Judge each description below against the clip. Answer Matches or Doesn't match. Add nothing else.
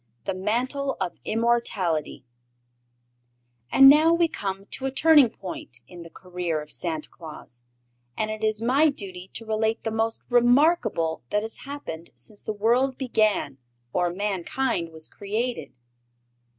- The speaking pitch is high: Matches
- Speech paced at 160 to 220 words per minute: Doesn't match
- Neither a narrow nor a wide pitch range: Doesn't match